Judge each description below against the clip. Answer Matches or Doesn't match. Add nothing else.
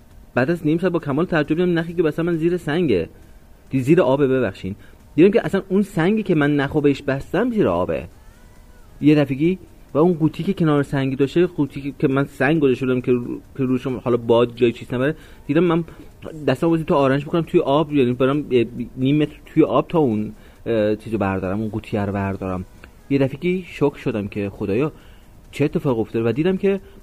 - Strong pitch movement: Matches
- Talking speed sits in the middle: Doesn't match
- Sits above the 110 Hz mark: Matches